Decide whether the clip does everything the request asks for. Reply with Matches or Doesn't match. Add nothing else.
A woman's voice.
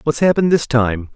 Doesn't match